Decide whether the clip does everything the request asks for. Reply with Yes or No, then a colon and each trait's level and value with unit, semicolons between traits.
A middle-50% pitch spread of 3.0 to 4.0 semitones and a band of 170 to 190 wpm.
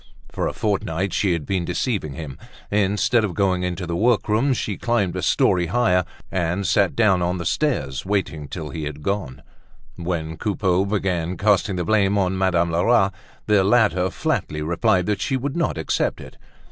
Yes: average, 3.4 semitones; average, 180 wpm